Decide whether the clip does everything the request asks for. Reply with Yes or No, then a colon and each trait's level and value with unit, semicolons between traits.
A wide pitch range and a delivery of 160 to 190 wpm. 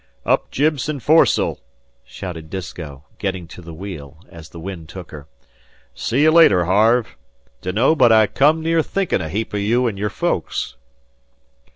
Yes: wide, 7.3 semitones; average, 165 wpm